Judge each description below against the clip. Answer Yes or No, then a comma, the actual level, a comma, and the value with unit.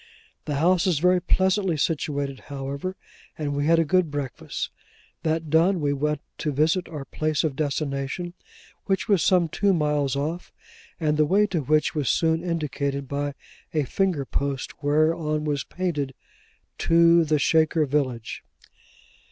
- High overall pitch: No, medium, 155 Hz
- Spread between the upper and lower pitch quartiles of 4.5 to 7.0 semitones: No, average, 2.9 semitones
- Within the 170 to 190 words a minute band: No, average, 150 wpm